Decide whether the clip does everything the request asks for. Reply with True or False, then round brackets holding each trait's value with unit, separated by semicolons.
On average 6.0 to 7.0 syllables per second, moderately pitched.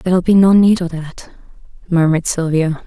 False (5.4 syllables/s; 175 Hz)